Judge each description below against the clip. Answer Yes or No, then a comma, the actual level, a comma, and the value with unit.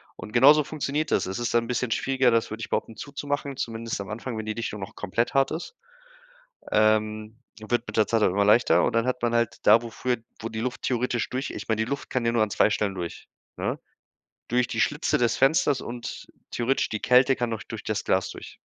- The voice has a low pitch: Yes, low, 115 Hz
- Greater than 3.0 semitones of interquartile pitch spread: No, average, 2.7 semitones